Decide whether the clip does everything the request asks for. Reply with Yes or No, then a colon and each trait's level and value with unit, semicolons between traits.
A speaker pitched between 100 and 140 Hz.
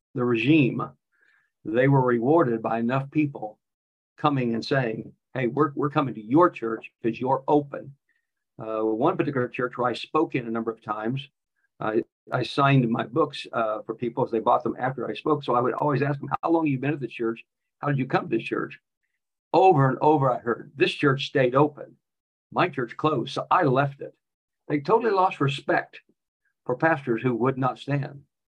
Yes: low, 135 Hz